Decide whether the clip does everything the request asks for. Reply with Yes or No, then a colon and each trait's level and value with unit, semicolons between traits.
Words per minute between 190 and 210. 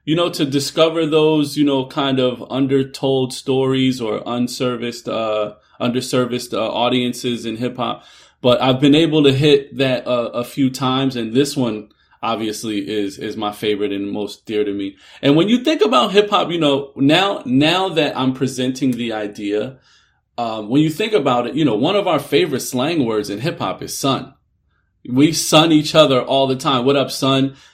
Yes: average, 195 wpm